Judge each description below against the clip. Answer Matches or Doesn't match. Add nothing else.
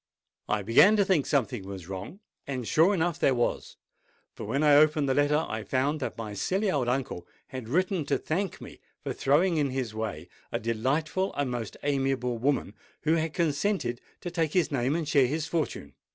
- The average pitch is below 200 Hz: Matches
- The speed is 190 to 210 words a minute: Matches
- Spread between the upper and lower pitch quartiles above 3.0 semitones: Matches